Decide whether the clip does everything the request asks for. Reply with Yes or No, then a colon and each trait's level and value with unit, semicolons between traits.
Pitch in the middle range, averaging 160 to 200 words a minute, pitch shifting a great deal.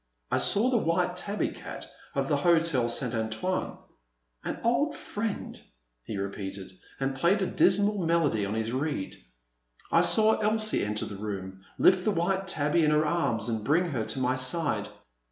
Yes: medium, 160 Hz; average, 170 wpm; wide, 9.0 semitones